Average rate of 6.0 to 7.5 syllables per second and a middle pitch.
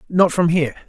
Yes: 6.7 syllables/s; medium, 165 Hz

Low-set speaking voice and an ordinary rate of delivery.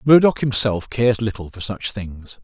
Yes: low, 110 Hz; average, 175 wpm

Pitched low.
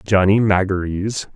Yes: low, 100 Hz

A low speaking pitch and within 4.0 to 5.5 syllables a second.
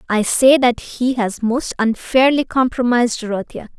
No: high, 240 Hz; 4.7 syllables/s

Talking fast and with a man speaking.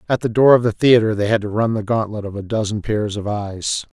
Yes: fast, 270 wpm; male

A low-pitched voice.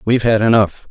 Yes: low, 110 Hz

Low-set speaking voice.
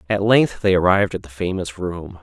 Yes: very low, 95 Hz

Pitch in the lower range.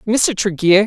No: high, 205 Hz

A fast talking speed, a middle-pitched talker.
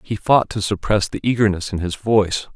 No: fast, 210 wpm; low, 100 Hz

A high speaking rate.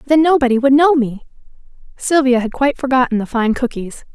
No: average, 175 wpm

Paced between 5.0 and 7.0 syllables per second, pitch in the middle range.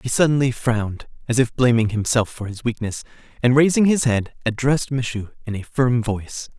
No: 5.5 syllables/s; low, 120 Hz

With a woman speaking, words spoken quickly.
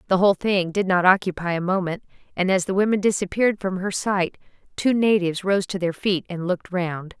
Yes: female; fast, 210 wpm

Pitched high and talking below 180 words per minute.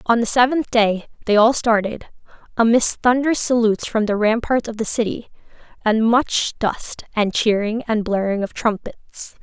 Yes: high, 225 Hz; average, 160 wpm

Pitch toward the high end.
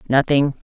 No: medium, 140 Hz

